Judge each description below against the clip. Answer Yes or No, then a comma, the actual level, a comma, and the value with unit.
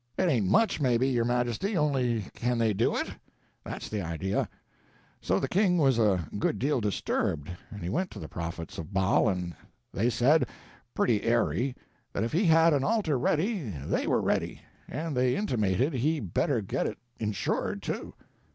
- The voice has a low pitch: Yes, low, 120 Hz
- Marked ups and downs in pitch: Yes, wide, 6.8 semitones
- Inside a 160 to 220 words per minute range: Yes, average, 175 wpm